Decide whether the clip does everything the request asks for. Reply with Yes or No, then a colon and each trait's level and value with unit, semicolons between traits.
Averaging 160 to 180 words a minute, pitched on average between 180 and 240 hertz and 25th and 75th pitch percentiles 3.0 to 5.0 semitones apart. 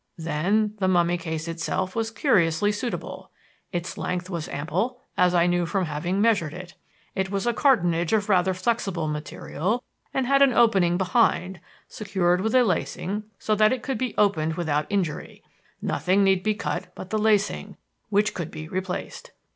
Yes: average, 170 wpm; high, 190 Hz; average, 3.8 semitones